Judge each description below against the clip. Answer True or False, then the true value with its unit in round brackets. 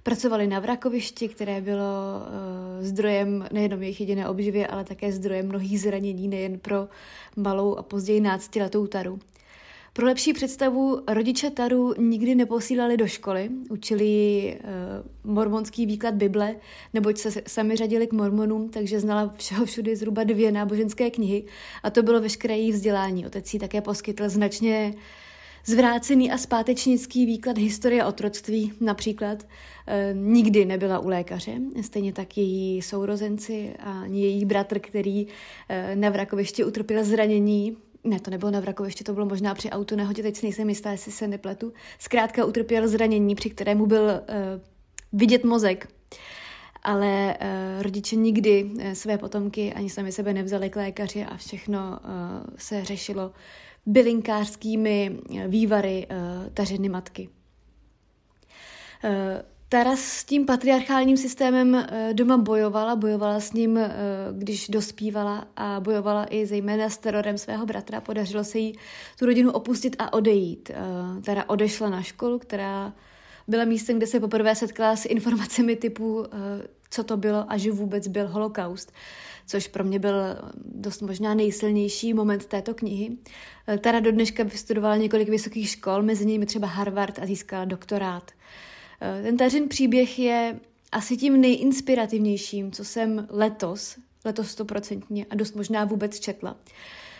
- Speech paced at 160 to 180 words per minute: False (135 wpm)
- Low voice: False (210 Hz)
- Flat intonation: True (1.9 semitones)